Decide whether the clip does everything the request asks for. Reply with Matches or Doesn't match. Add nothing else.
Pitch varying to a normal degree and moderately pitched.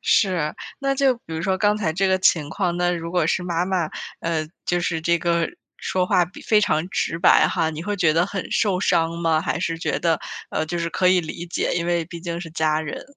Doesn't match